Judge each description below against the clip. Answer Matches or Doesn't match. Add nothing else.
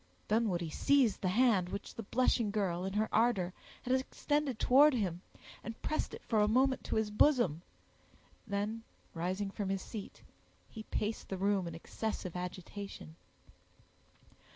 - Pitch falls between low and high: Doesn't match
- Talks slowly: Doesn't match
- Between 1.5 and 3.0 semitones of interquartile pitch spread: Doesn't match